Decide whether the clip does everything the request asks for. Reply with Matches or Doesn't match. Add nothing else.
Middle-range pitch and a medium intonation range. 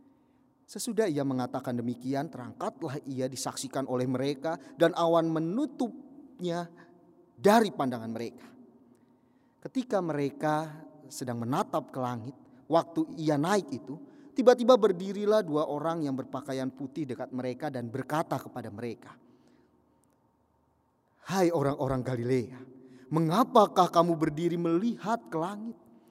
Doesn't match